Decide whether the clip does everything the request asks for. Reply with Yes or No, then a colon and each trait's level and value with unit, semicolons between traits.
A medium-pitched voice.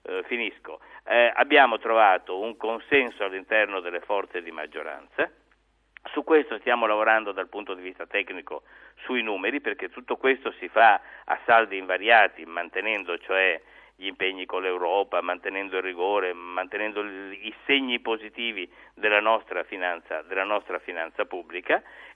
No: low, 105 Hz